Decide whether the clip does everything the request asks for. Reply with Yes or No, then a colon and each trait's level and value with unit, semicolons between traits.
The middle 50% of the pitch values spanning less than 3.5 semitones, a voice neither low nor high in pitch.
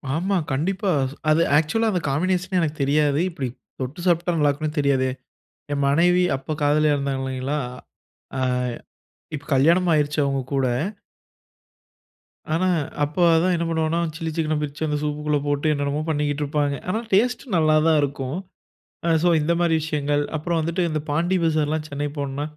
Yes: average, 2.8 semitones; medium, 150 Hz